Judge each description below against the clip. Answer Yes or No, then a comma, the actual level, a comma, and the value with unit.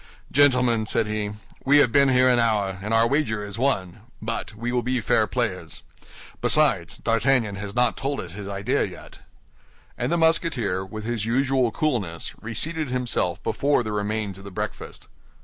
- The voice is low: Yes, low, 115 Hz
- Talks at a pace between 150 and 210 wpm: Yes, average, 170 wpm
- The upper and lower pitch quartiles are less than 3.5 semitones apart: No, average, 4.2 semitones